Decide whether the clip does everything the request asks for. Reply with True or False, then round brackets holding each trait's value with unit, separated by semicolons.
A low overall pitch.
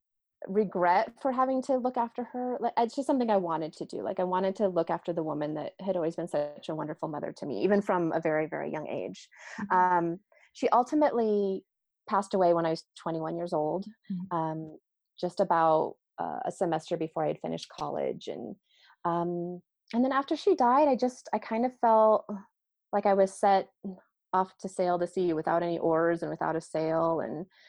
False (185 Hz)